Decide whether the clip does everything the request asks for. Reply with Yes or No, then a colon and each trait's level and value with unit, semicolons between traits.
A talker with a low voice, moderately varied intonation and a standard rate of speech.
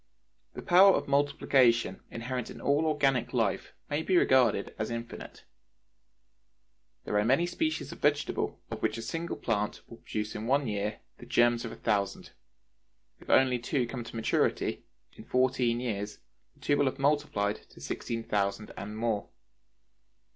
Yes: low, 120 Hz; average, 4.7 semitones; average, 160 wpm